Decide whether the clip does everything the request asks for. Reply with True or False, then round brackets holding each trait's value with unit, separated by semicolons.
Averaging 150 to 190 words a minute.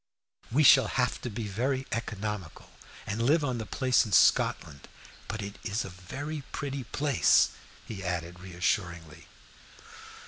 False (140 wpm)